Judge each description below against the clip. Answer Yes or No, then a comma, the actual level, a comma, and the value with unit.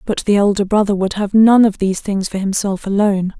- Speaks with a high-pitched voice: Yes, high, 200 Hz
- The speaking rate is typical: No, fast, 230 wpm